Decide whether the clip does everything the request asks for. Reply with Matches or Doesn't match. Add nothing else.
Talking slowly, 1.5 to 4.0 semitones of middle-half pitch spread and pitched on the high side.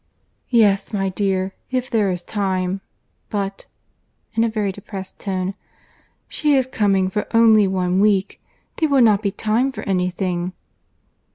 Matches